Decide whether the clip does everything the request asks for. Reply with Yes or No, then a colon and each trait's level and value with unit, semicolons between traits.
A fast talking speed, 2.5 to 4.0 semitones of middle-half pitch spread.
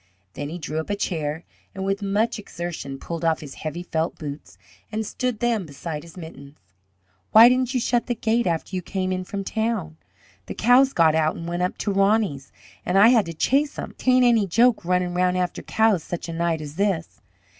No: fast, 210 wpm; average, 5.3 semitones